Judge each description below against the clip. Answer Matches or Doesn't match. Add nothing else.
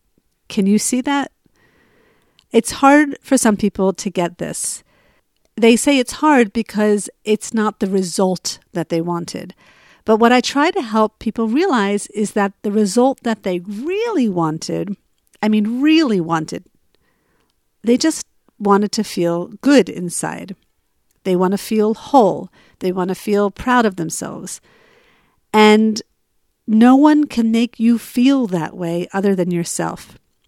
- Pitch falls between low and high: Doesn't match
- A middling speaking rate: Matches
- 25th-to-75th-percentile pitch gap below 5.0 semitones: Matches